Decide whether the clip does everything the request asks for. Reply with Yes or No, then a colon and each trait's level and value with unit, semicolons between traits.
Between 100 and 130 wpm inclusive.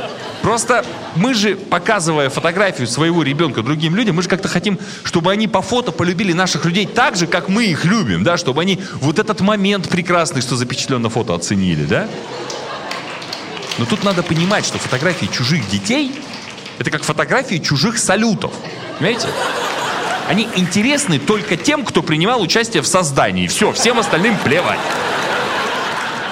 No: average, 150 wpm